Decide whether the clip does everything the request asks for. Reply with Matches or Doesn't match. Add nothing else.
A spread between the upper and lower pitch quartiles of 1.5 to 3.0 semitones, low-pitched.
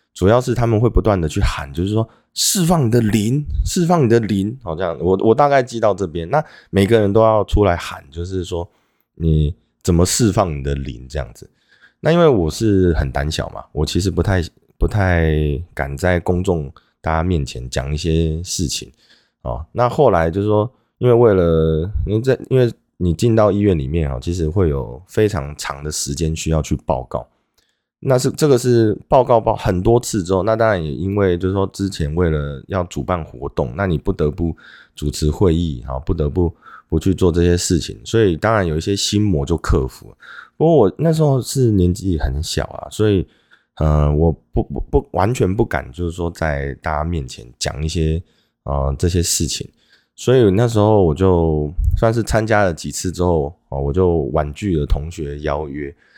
Doesn't match